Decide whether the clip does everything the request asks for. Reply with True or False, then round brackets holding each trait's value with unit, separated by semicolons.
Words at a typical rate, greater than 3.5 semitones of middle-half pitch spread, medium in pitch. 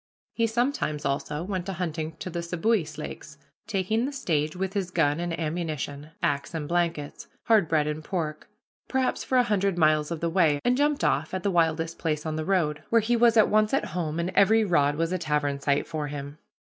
False (210 wpm; 4.5 semitones; 170 Hz)